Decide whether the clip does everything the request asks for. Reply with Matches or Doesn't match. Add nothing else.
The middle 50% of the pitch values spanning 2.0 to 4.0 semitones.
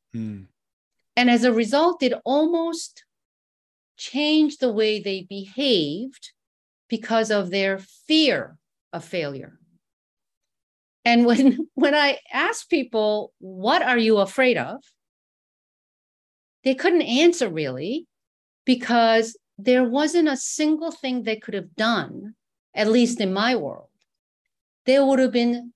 Doesn't match